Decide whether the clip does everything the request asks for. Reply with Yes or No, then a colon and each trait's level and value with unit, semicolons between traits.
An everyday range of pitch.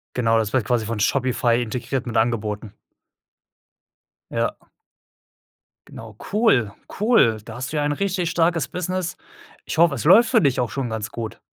No: wide, 6.9 semitones